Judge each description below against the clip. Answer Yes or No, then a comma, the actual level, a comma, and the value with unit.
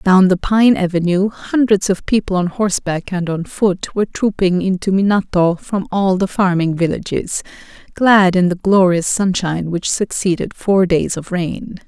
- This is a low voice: No, high, 190 Hz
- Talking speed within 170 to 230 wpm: No, average, 160 wpm